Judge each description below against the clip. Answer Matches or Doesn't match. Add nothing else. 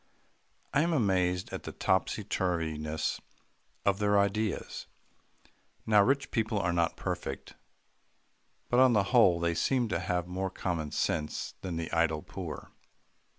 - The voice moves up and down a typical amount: Matches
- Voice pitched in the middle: Doesn't match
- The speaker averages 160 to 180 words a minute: Doesn't match